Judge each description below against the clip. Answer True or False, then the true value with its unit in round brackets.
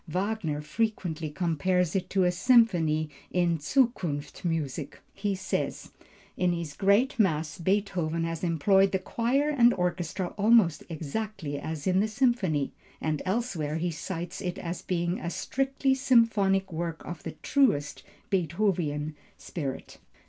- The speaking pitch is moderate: True (180 Hz)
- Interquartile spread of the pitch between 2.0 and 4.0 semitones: False (4.5 semitones)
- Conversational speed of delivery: False (130 wpm)